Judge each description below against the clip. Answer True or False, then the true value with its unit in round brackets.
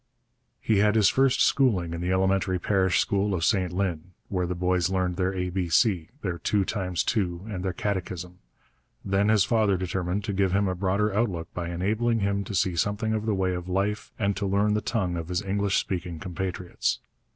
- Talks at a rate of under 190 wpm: False (205 wpm)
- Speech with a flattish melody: True (2.3 semitones)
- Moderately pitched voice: False (95 Hz)